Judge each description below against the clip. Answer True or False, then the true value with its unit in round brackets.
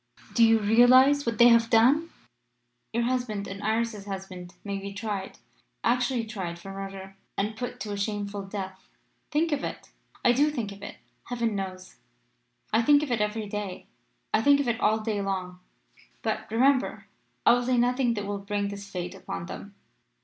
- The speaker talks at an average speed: True (180 wpm)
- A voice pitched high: True (215 Hz)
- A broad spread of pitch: False (3.4 semitones)